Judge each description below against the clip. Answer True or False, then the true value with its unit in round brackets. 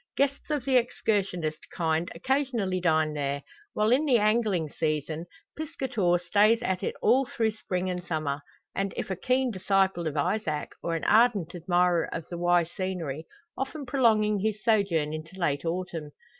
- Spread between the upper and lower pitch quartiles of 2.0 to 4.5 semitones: False (5.2 semitones)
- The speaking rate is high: False (160 wpm)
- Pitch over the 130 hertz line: True (185 Hz)